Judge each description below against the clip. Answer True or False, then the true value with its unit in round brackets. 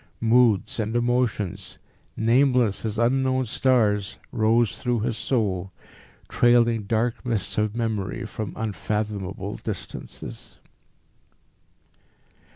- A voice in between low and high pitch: False (110 Hz)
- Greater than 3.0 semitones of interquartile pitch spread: False (2.6 semitones)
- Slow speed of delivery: True (90 wpm)